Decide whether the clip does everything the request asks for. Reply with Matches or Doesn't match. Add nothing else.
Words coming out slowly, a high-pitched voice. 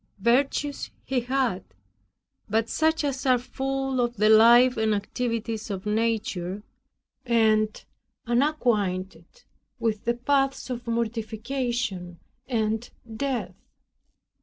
Matches